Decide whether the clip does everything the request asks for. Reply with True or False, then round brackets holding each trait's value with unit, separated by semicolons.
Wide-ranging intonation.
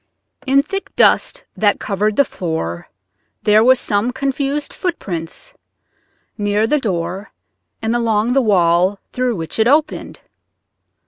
True (5.9 semitones)